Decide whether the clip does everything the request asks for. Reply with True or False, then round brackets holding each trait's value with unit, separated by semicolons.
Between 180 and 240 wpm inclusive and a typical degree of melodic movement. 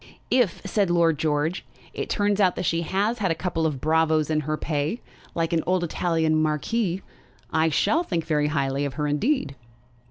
True (185 wpm; 3.4 semitones)